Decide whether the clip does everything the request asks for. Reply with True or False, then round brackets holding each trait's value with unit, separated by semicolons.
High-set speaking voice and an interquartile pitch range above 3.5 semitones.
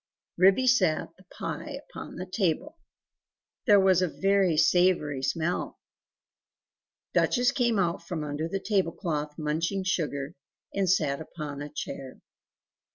False (175 Hz; 4.2 semitones)